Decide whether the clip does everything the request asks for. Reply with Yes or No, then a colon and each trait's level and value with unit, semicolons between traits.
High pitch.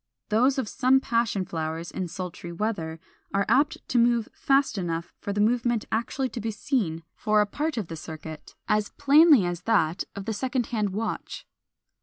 Yes: high, 215 Hz